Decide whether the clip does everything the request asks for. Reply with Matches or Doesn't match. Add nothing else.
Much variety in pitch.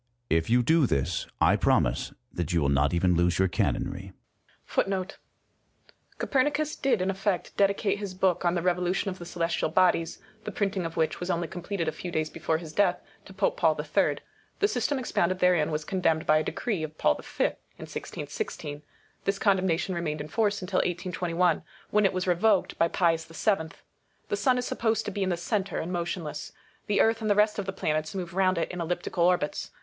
Doesn't match